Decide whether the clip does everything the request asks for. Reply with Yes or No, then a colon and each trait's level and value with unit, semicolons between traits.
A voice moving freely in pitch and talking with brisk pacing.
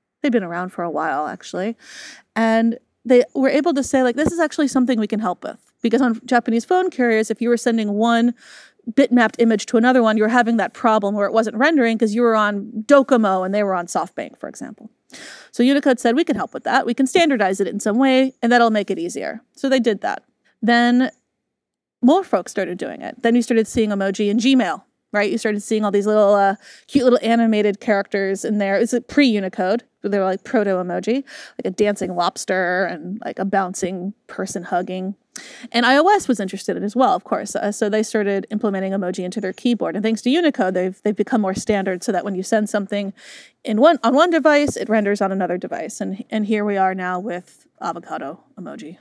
No: average, 3.8 semitones; fast, 220 wpm